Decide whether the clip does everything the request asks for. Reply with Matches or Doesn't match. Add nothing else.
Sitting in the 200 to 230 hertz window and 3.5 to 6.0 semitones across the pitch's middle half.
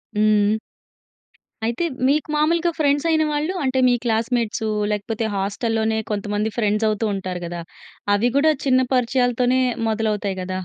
Matches